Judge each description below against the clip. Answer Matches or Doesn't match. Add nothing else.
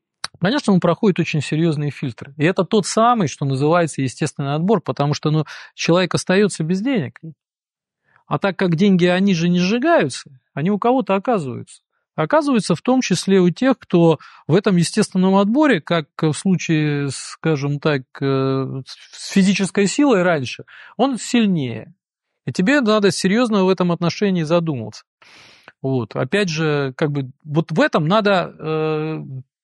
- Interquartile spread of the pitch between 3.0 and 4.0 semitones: Doesn't match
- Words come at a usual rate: Matches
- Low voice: Doesn't match